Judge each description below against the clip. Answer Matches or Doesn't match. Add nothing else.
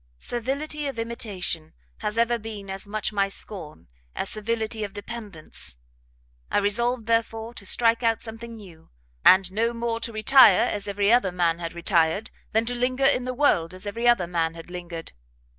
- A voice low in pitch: Doesn't match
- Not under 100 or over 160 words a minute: Doesn't match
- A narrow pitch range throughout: Doesn't match